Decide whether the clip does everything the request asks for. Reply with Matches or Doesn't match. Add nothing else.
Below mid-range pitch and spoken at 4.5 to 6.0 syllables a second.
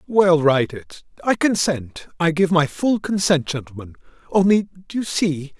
Doesn't match